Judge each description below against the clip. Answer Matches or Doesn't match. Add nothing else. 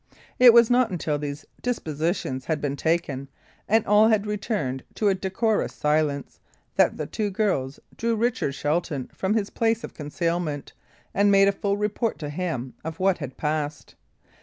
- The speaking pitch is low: Doesn't match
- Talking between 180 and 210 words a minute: Doesn't match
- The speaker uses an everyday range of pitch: Doesn't match